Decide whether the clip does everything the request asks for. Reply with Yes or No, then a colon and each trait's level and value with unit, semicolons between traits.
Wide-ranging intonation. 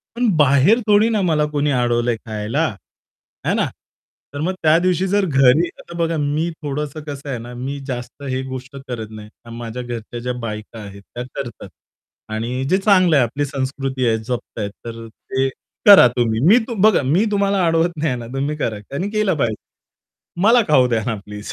Yes: wide, 5.9 semitones